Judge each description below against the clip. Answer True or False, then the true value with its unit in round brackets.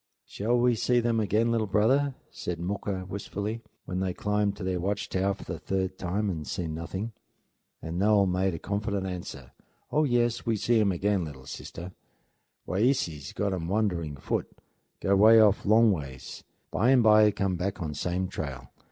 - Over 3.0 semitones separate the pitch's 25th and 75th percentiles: True (3.4 semitones)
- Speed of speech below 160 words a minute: False (170 wpm)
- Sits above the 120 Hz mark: False (100 Hz)